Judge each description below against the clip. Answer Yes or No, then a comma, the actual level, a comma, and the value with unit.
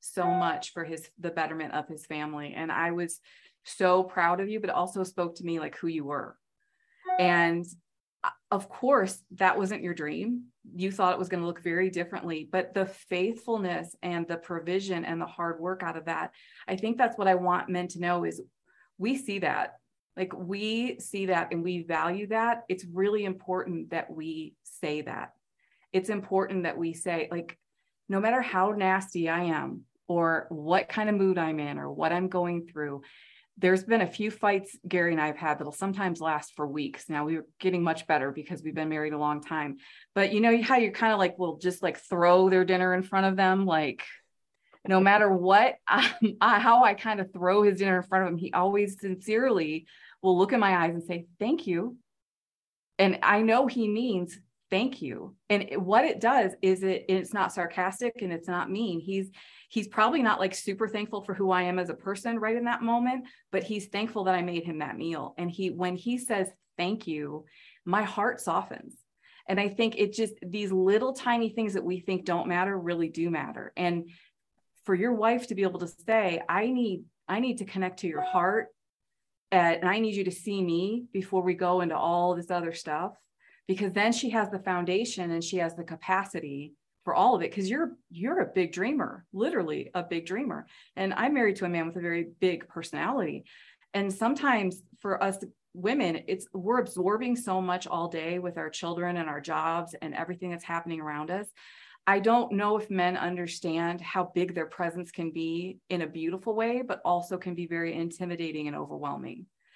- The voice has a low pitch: No, medium, 185 Hz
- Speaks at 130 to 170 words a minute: No, fast, 205 wpm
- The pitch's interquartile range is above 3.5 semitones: No, average, 3.1 semitones